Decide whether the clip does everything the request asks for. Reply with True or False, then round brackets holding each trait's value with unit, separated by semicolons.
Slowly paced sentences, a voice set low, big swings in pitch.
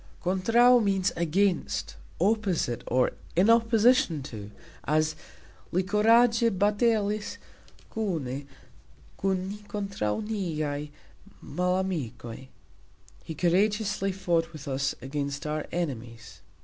False (95 wpm; 180 Hz; 6.2 semitones)